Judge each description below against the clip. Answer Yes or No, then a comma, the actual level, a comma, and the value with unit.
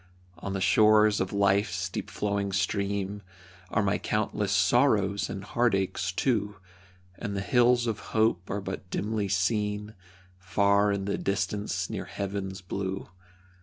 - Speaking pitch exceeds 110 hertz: No, low, 100 Hz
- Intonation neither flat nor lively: No, narrow, 1.5 semitones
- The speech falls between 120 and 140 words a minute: Yes, slow, 135 wpm